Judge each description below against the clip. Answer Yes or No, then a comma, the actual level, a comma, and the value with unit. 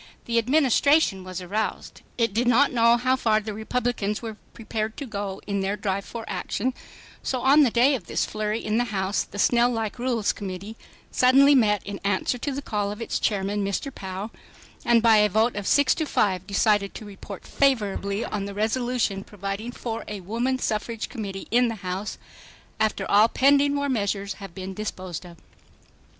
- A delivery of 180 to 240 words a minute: Yes, average, 185 wpm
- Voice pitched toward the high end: Yes, high, 215 Hz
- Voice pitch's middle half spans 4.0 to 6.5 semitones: No, average, 3.4 semitones